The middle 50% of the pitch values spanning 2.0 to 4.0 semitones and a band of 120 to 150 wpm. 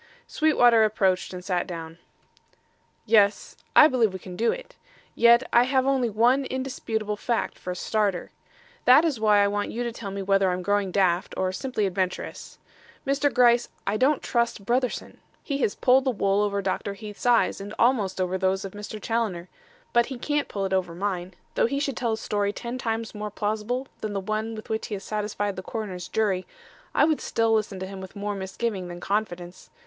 No: average, 3.7 semitones; average, 200 wpm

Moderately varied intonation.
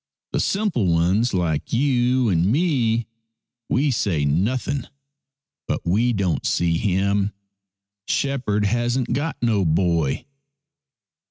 No: wide, 5.9 semitones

